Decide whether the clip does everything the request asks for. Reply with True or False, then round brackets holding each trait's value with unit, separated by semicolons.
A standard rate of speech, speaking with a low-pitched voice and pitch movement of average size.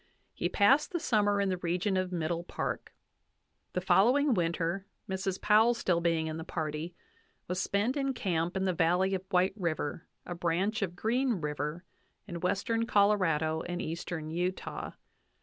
False (165 wpm; 180 Hz; 3.4 semitones)